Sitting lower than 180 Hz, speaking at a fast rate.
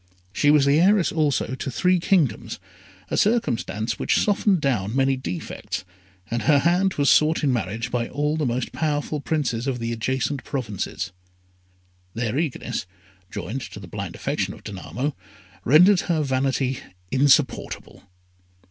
No: low, 135 Hz; average, 140 wpm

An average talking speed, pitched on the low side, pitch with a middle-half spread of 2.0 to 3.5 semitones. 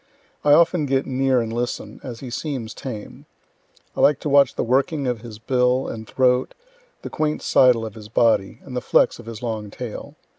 Yes: average, 190 wpm; low, 125 Hz; average, 3.0 semitones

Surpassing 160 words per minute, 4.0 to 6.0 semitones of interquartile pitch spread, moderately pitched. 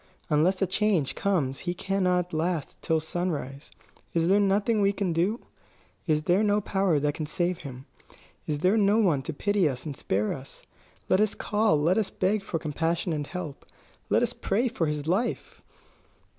Yes: average, 180 wpm; average, 4.6 semitones; medium, 175 Hz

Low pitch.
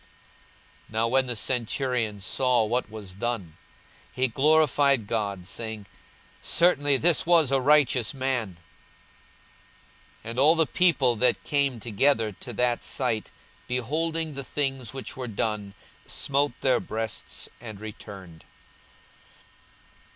Yes: low, 125 Hz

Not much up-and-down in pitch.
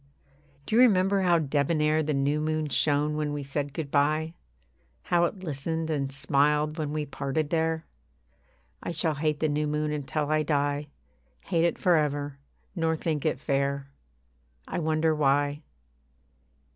Yes: narrow, 1.9 semitones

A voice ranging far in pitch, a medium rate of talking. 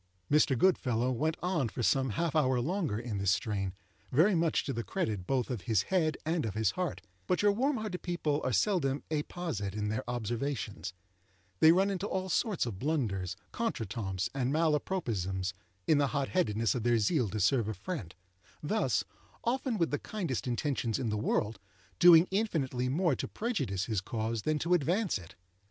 Yes: wide, 8.2 semitones; average, 180 wpm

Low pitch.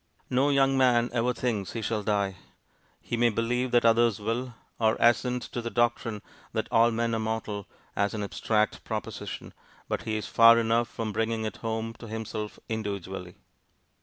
Yes: low, 115 Hz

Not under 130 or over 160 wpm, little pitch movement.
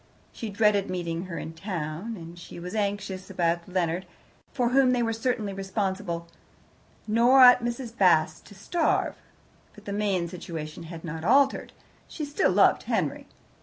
No: average, 155 wpm; average, 5.0 semitones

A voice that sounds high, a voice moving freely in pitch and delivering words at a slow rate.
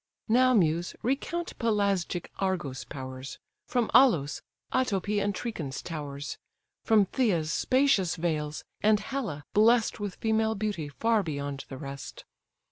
Yes: high, 195 Hz; wide, 6.9 semitones; slow, 125 wpm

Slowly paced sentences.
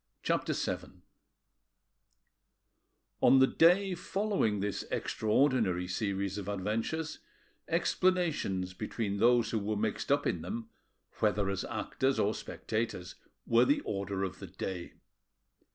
Yes: slow, 120 wpm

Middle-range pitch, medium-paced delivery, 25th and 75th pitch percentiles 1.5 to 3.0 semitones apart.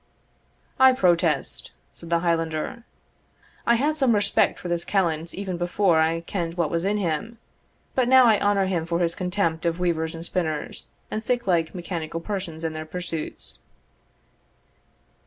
No: medium, 175 Hz; average, 155 wpm; average, 3.6 semitones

